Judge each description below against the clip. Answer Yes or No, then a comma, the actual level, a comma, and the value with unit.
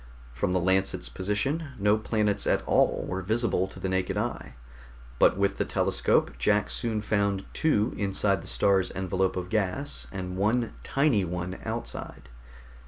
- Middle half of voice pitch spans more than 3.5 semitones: No, narrow, 2.5 semitones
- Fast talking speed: No, average, 155 wpm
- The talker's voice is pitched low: Yes, low, 100 Hz